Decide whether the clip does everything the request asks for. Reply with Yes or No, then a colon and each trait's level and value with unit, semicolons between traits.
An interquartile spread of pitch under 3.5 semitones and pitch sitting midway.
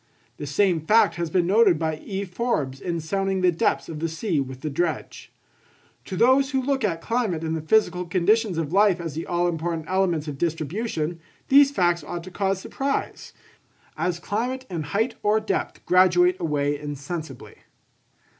No: average, 4.3 semitones; medium, 175 Hz